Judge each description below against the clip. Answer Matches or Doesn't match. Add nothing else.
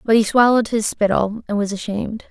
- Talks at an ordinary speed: Doesn't match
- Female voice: Matches